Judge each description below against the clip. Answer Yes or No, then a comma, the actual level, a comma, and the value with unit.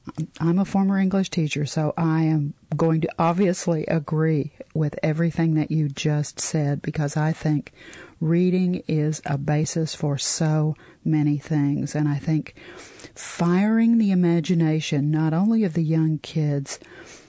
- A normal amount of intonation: No, narrow, 2.0 semitones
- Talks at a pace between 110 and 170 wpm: Yes, average, 140 wpm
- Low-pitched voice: No, medium, 155 Hz